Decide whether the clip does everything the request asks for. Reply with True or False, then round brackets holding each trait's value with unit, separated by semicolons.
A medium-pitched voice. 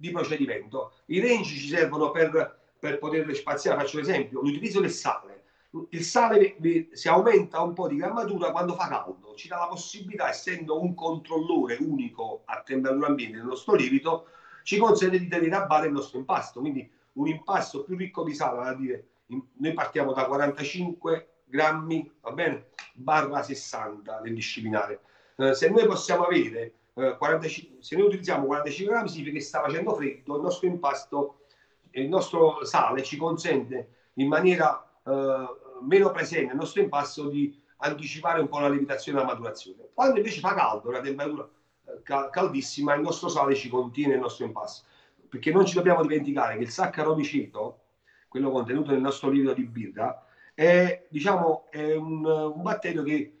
True (155 Hz)